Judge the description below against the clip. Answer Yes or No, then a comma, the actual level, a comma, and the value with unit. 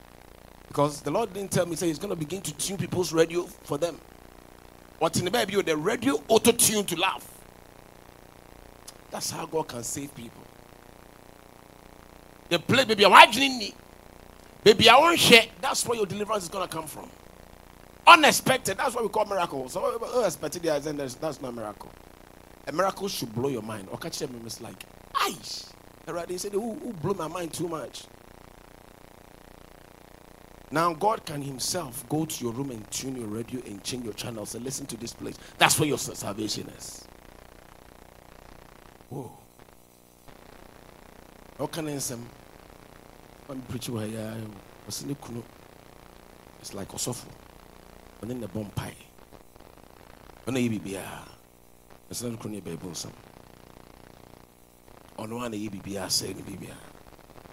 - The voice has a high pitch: No, low, 115 Hz